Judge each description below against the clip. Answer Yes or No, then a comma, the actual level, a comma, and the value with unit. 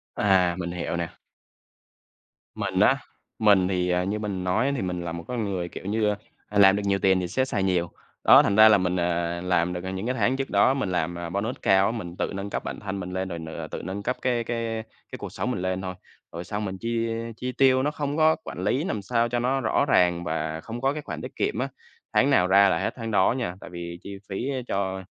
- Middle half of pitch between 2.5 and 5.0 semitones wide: Yes, average, 4.4 semitones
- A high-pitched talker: No, very low, 95 Hz